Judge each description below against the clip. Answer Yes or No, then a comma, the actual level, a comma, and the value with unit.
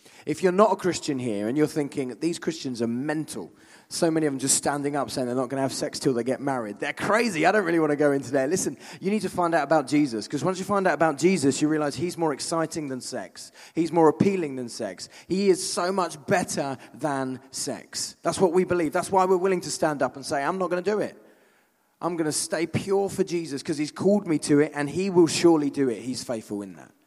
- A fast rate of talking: Yes, fast, 260 wpm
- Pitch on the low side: No, medium, 155 Hz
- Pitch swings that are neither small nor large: Yes, average, 4.5 semitones